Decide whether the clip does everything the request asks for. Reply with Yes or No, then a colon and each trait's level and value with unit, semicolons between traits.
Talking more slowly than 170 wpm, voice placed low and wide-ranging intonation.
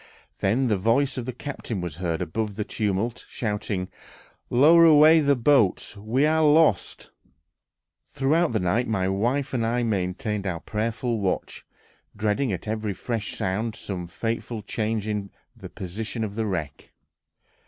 No: average, 150 wpm; low, 110 Hz; average, 4.1 semitones